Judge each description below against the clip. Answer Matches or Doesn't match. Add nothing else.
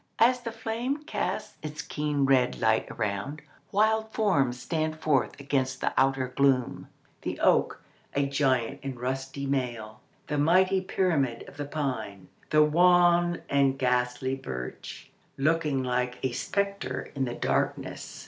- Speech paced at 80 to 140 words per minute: Matches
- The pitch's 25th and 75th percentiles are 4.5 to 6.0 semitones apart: Matches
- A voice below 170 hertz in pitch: Matches